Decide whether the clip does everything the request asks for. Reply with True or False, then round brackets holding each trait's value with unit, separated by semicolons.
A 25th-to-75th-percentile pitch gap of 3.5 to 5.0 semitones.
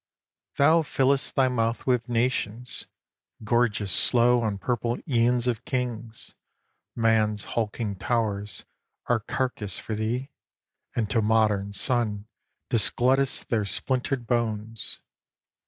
False (2.5 semitones)